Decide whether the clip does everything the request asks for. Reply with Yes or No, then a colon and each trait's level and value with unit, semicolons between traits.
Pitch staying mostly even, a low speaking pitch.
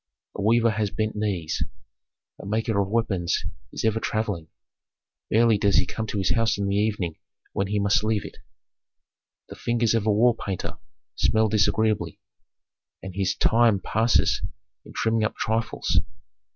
Yes: narrow, 2.0 semitones; low, 110 Hz